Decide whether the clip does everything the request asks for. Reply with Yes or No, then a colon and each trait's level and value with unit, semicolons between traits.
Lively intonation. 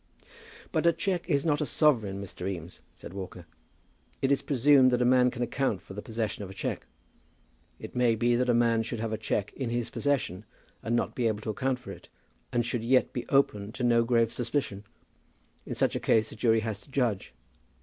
No: average, 3.1 semitones